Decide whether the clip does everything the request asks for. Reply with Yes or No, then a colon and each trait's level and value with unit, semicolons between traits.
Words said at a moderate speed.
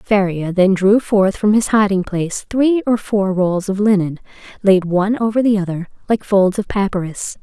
Yes: average, 185 wpm